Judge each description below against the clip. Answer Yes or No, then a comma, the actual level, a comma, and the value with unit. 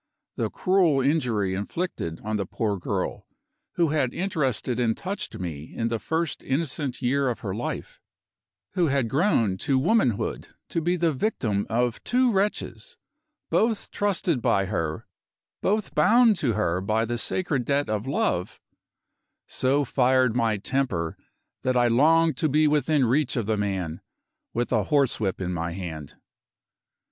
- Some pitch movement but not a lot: No, wide, 7.2 semitones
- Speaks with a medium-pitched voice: No, low, 130 Hz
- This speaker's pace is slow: No, average, 150 wpm